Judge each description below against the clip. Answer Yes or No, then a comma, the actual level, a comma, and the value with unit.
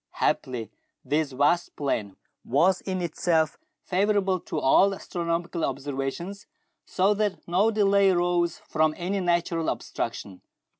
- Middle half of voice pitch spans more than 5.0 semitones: No, average, 3.8 semitones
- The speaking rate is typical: No, slow, 115 wpm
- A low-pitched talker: No, medium, 175 Hz